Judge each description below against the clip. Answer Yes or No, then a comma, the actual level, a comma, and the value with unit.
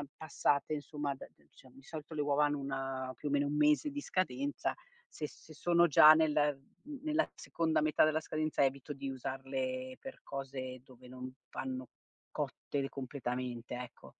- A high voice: No, medium, 145 Hz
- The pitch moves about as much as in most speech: Yes, average, 3.0 semitones